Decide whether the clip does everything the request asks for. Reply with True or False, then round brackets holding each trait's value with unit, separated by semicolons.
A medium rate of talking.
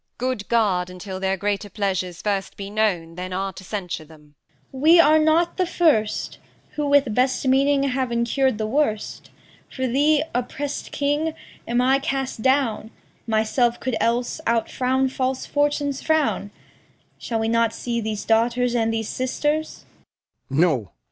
True (150 wpm)